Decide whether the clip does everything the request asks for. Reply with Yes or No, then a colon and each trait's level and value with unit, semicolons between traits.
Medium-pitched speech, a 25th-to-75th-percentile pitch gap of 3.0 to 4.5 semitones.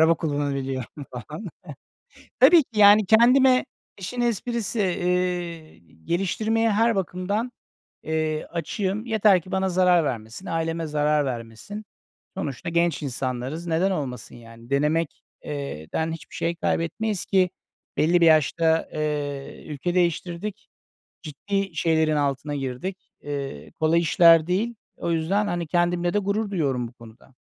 No: medium, 165 Hz; average, 4.9 semitones